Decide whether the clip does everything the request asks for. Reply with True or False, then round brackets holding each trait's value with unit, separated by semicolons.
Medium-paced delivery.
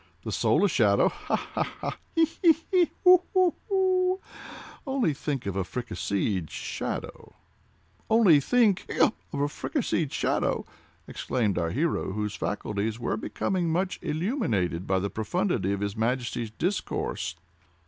False (130 wpm)